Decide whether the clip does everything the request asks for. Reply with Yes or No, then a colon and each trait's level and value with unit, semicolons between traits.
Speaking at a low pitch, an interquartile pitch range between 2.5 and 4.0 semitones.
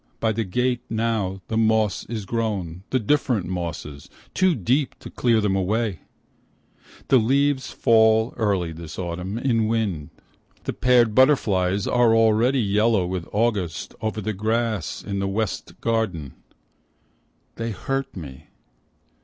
Yes: low, 110 Hz; average, 3.7 semitones